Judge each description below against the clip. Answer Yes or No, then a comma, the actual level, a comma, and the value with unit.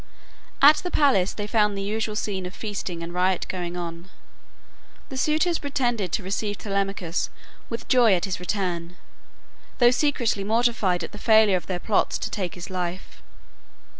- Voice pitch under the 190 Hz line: No, high, 200 Hz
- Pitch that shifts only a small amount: No, average, 4.1 semitones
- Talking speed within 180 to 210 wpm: No, average, 165 wpm